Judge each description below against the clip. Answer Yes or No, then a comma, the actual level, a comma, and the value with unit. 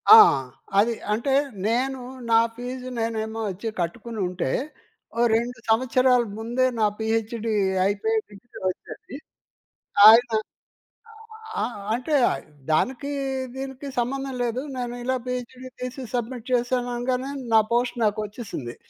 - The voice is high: Yes, high, 240 Hz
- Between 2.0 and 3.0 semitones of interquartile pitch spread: Yes, narrow, 2.4 semitones